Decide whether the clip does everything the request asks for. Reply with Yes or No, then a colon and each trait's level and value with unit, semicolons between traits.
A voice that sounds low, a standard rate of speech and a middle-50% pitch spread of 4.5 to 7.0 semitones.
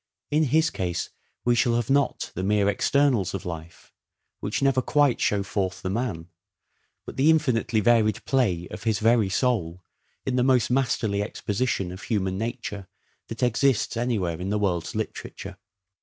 Yes: low, 110 Hz; average, 160 wpm; average, 5.0 semitones